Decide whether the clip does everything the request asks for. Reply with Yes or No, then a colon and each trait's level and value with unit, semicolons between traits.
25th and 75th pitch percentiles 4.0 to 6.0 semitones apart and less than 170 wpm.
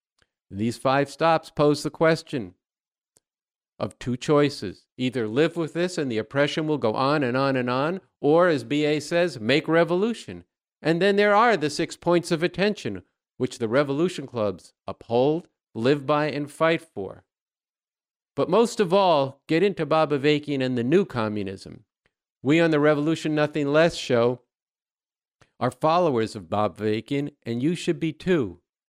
Yes: average, 4.8 semitones; average, 160 wpm